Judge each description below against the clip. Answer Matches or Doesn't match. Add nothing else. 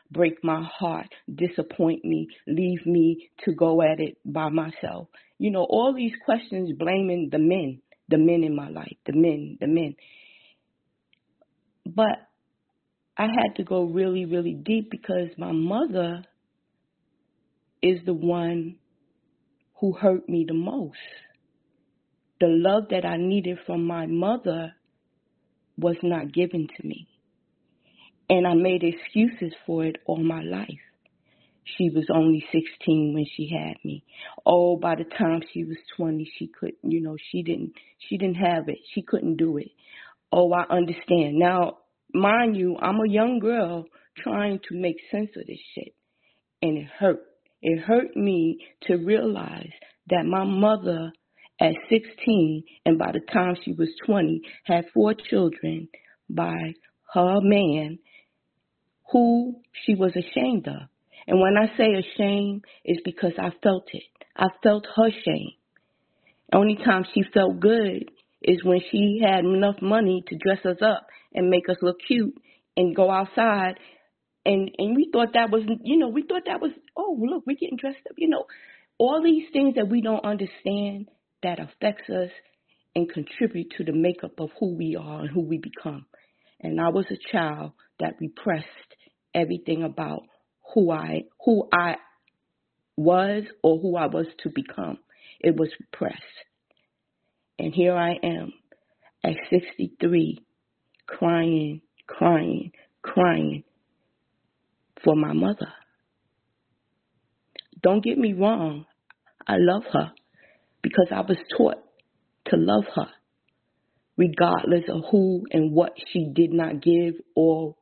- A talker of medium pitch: Matches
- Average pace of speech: Matches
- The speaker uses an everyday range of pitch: Matches